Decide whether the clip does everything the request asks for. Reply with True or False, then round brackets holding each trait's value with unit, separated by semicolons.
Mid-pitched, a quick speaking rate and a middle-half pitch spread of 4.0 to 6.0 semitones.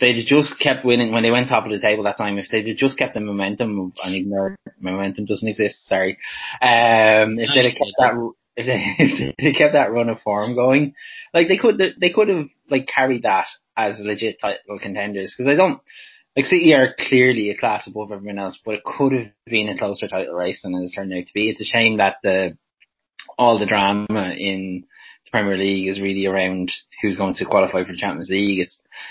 False (105 Hz; 220 wpm; 4.5 semitones)